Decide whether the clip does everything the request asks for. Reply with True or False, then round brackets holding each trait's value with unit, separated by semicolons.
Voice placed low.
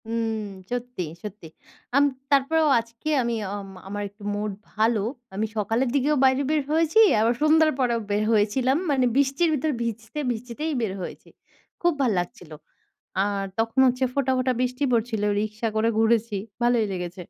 False (235 Hz)